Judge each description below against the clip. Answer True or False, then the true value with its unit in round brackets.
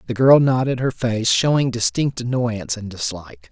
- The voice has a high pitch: False (120 Hz)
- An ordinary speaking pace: True (170 wpm)